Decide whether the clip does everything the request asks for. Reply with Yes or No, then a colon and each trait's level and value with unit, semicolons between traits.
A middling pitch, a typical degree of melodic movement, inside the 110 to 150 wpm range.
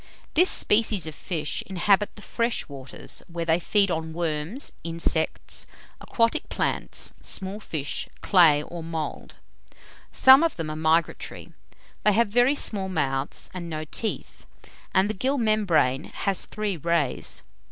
Yes: medium, 175 Hz; average, 5.0 semitones; average, 140 wpm